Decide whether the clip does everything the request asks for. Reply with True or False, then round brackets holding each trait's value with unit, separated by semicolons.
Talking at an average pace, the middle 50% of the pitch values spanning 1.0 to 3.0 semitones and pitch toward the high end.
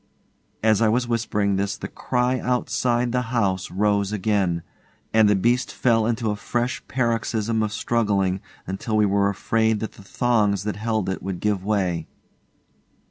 False (160 wpm; 2.7 semitones; 110 Hz)